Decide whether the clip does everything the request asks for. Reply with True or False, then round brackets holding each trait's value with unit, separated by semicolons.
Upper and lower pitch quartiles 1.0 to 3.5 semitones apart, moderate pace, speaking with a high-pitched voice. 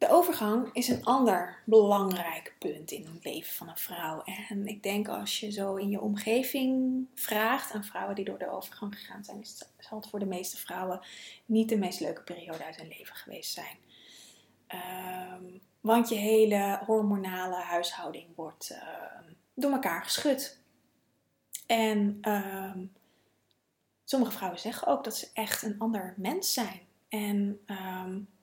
True (3.2 semitones; 155 wpm; 205 Hz)